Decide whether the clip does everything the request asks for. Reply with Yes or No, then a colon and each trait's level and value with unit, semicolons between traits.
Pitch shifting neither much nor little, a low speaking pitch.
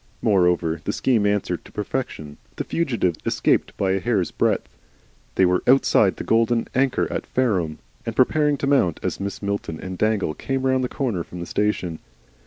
No: wide, 6.3 semitones; low, 105 Hz